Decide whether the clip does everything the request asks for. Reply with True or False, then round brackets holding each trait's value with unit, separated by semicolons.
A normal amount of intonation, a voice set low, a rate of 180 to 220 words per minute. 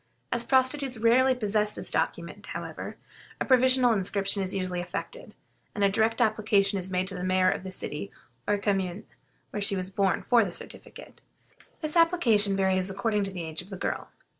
False (3.6 semitones; 200 Hz; 185 wpm)